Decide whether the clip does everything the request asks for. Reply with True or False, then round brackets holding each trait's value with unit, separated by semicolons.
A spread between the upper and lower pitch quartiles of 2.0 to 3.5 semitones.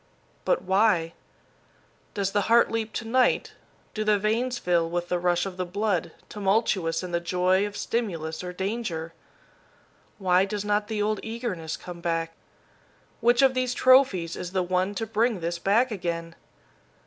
False (4.1 semitones)